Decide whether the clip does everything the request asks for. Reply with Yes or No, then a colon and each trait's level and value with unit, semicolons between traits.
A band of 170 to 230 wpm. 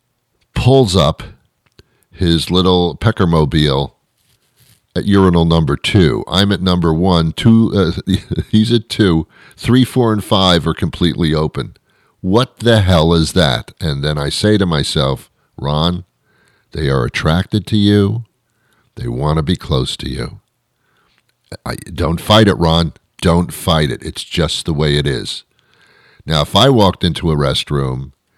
No: average, 150 wpm